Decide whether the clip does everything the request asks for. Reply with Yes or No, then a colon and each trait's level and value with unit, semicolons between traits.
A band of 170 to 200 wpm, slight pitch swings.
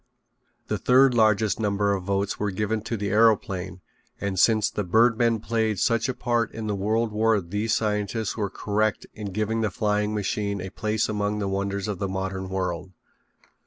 Yes: average, 180 wpm; narrow, 2.0 semitones